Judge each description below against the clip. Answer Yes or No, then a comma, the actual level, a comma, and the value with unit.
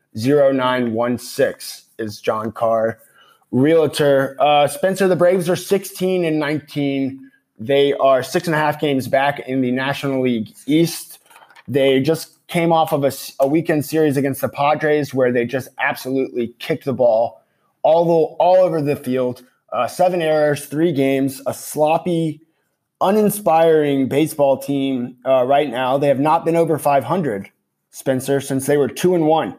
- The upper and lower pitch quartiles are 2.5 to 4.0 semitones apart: Yes, average, 3.3 semitones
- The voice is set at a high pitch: No, medium, 140 Hz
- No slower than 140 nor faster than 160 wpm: Yes, average, 155 wpm